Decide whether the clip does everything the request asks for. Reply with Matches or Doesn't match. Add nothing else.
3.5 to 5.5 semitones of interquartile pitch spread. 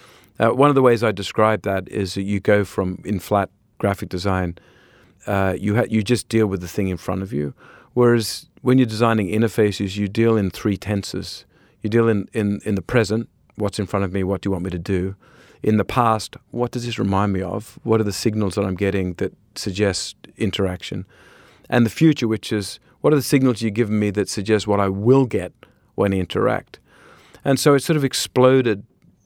Doesn't match